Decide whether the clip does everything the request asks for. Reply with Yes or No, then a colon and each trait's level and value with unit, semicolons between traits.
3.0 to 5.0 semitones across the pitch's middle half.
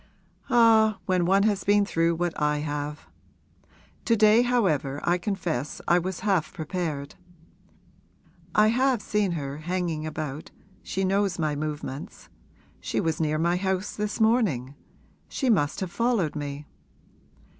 No: wide, 5.4 semitones